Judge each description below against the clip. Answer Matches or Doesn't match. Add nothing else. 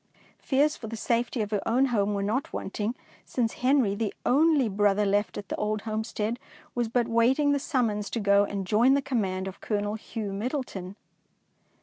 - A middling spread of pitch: Matches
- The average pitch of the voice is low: Doesn't match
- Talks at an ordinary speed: Matches